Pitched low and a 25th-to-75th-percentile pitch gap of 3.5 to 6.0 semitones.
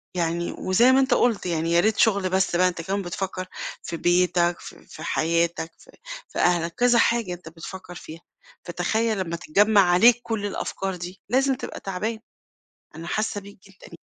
No: medium, 185 Hz; average, 3.9 semitones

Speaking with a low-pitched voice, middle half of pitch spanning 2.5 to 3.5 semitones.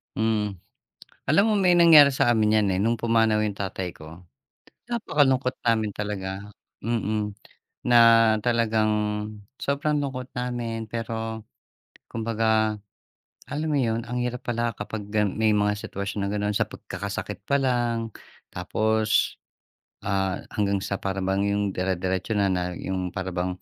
Yes: low, 110 Hz; average, 2.9 semitones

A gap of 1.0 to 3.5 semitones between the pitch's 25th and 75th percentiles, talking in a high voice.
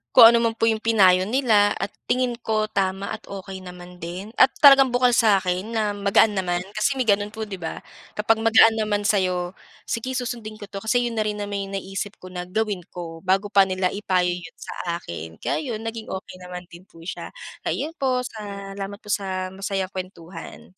Yes: average, 3.1 semitones; high, 200 Hz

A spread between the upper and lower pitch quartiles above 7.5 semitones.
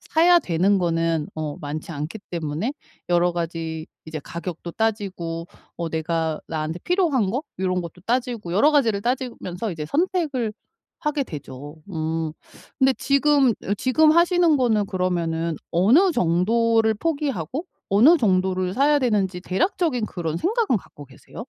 Yes: wide, 8.1 semitones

